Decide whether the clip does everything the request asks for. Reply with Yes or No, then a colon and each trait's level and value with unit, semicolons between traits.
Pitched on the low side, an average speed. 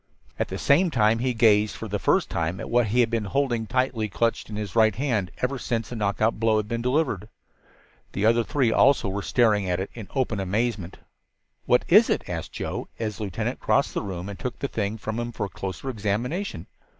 No: low, 110 Hz; fast, 220 wpm